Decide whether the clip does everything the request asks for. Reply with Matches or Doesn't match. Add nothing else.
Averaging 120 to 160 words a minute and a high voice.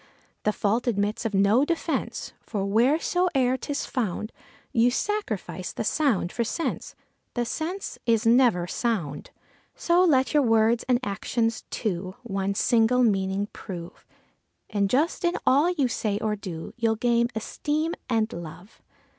Matches